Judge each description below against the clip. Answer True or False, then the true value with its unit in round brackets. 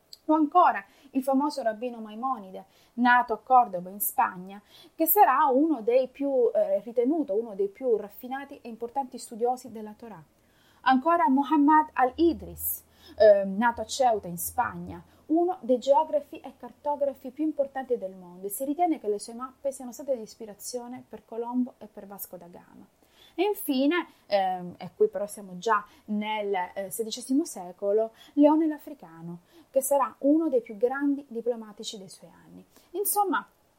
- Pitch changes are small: False (5.3 semitones)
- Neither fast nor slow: True (160 wpm)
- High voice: True (245 Hz)